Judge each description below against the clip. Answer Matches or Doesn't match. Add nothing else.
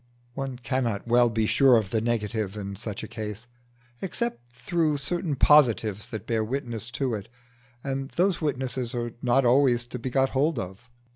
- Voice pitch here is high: Doesn't match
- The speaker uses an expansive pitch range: Doesn't match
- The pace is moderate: Matches